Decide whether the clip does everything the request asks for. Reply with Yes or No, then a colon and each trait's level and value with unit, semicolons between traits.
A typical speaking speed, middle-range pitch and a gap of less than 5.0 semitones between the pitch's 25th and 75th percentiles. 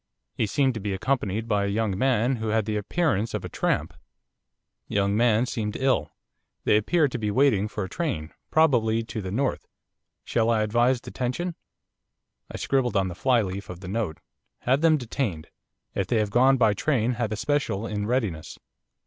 No: average, 185 wpm; low, 110 Hz; average, 4.1 semitones